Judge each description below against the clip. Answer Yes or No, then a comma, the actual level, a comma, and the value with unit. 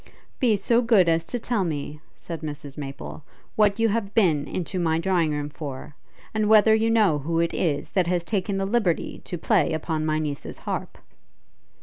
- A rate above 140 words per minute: Yes, average, 190 wpm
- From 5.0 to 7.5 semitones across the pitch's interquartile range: Yes, wide, 5.4 semitones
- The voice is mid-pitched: Yes, medium, 175 Hz